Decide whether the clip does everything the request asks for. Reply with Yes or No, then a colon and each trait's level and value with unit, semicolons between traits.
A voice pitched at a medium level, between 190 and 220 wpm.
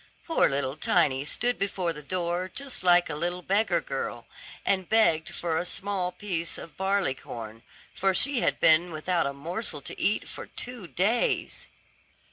No: medium, 180 Hz; average, 165 wpm